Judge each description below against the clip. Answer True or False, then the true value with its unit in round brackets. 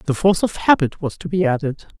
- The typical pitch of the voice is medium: True (180 Hz)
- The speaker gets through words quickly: True (240 wpm)